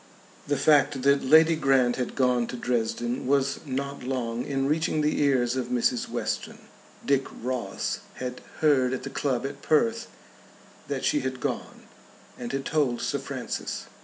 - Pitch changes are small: Yes, narrow, 2.2 semitones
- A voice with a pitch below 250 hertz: Yes, low, 135 Hz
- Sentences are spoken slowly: No, average, 160 wpm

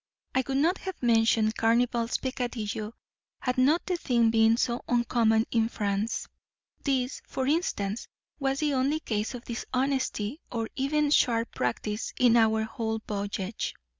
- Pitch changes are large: No, average, 3.1 semitones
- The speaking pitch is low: No, high, 235 Hz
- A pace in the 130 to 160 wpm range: Yes, average, 140 wpm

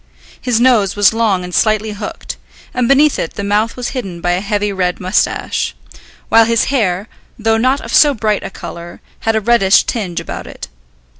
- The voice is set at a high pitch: Yes, high, 215 Hz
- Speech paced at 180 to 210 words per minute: Yes, average, 190 wpm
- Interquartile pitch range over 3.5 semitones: No, average, 3.2 semitones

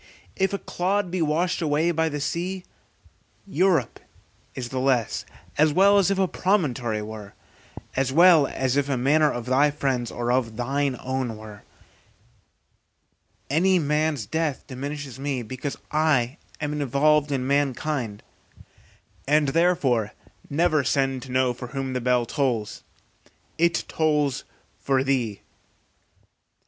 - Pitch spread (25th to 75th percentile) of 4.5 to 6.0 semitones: No, average, 3.8 semitones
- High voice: No, medium, 140 Hz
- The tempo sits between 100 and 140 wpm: Yes, slow, 135 wpm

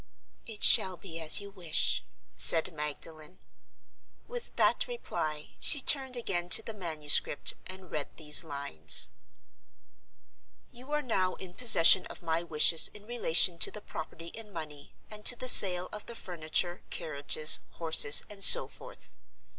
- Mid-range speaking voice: Yes, medium, 175 Hz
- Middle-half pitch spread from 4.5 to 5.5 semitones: Yes, average, 5.2 semitones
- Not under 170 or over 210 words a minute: No, average, 150 wpm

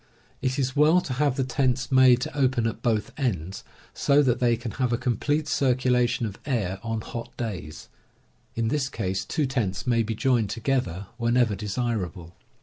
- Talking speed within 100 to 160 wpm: No, average, 180 wpm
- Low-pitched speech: Yes, low, 120 Hz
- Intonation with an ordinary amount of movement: Yes, average, 3.2 semitones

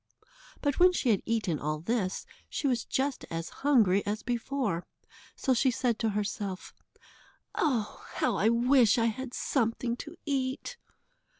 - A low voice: No, high, 235 Hz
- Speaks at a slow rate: No, average, 145 wpm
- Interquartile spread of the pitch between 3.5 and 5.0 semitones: Yes, average, 4.2 semitones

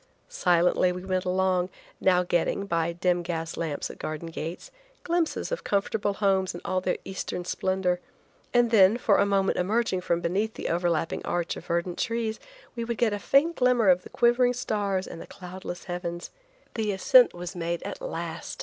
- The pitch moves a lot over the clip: No, average, 3.7 semitones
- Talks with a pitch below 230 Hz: Yes, medium, 185 Hz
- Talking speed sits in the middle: Yes, average, 180 wpm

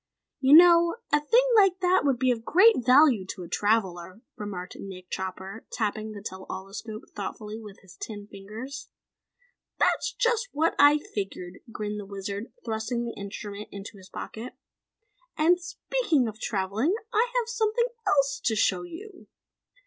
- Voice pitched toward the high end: Yes, high, 225 Hz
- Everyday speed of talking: Yes, average, 155 wpm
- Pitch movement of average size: No, wide, 8.0 semitones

